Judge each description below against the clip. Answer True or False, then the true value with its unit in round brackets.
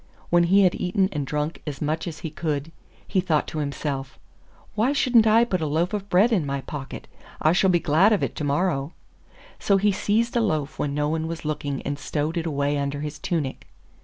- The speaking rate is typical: False (220 wpm)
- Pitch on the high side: False (160 Hz)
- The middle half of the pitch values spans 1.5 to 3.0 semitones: False (4.6 semitones)